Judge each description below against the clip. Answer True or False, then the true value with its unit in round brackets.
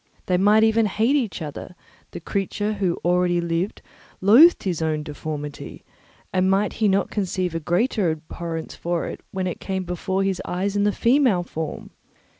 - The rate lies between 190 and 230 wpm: False (170 wpm)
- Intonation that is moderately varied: True (3.3 semitones)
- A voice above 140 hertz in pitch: True (185 Hz)